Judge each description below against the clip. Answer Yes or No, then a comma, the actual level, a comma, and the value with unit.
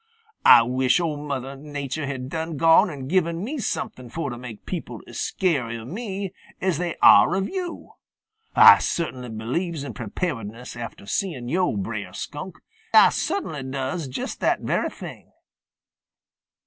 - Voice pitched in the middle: Yes, medium, 145 Hz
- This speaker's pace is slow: No, average, 150 wpm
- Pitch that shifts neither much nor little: No, wide, 5.7 semitones